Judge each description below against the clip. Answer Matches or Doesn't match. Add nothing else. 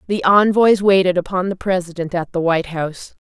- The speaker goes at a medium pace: Matches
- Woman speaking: Matches